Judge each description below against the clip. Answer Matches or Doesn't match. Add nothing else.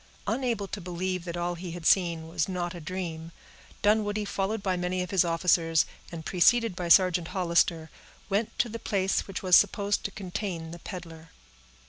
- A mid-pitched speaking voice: Matches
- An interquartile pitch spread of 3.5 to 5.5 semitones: Doesn't match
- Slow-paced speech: Doesn't match